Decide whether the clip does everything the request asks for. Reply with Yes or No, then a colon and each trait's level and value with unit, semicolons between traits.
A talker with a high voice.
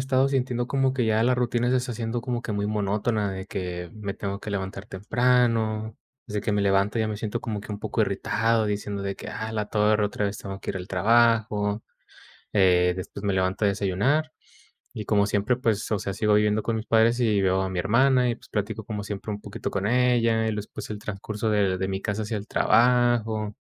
No: low, 105 Hz